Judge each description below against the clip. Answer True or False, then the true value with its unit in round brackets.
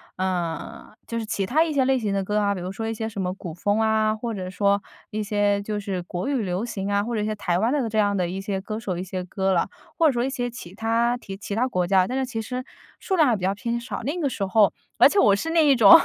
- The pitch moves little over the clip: False (3.6 semitones)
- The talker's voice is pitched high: True (210 Hz)